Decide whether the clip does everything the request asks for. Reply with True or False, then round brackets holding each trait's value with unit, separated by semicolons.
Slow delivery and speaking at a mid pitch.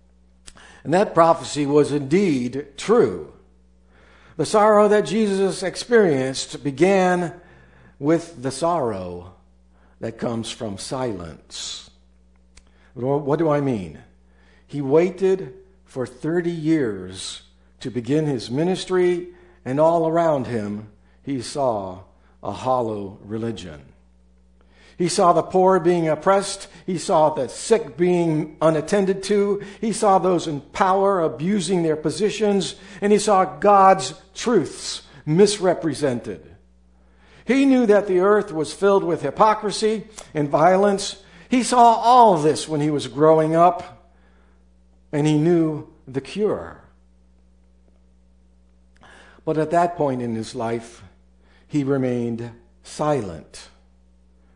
True (115 wpm; 145 Hz)